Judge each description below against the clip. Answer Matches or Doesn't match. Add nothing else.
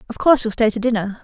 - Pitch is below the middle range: Doesn't match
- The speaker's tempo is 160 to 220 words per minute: Doesn't match